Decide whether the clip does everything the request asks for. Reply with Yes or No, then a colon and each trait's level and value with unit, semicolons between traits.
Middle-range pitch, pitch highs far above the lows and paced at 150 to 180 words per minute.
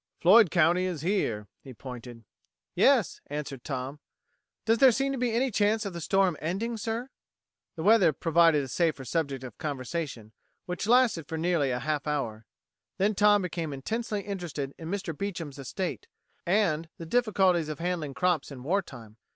Yes: medium, 170 Hz; wide, 6.1 semitones; average, 165 wpm